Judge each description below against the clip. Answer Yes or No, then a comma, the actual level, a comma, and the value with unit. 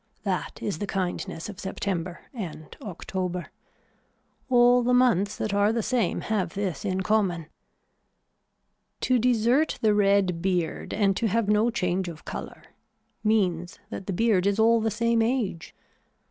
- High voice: Yes, high, 205 Hz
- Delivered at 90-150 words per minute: Yes, average, 145 wpm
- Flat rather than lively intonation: No, average, 3.7 semitones